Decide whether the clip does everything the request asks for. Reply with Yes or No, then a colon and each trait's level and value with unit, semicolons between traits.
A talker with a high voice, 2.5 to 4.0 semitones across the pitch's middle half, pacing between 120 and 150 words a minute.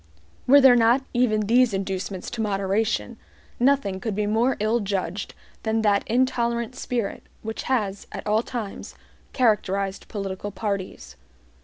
Yes: high, 215 Hz; average, 3.3 semitones; slow, 135 wpm